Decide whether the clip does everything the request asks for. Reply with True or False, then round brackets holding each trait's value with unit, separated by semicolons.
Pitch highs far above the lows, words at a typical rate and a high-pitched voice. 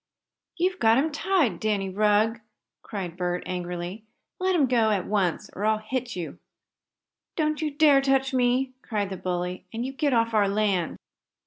True (5.9 semitones; 165 wpm; 220 Hz)